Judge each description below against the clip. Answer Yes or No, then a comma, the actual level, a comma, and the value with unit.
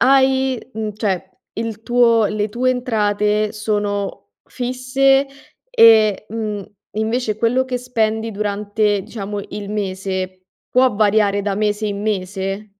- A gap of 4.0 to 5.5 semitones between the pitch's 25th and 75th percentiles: No, average, 2.7 semitones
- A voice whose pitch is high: Yes, high, 215 Hz